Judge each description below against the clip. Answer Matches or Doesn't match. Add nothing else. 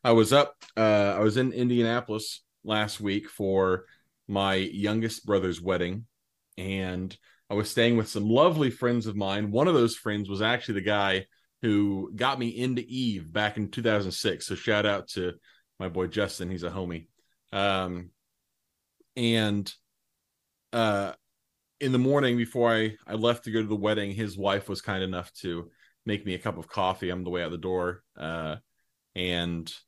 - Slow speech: Doesn't match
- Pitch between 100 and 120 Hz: Matches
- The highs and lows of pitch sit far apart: Doesn't match